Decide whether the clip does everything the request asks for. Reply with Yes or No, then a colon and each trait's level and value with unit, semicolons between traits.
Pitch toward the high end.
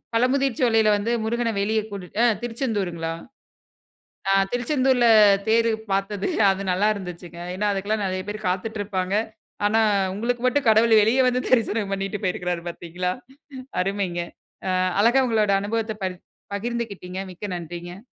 Yes: high, 210 Hz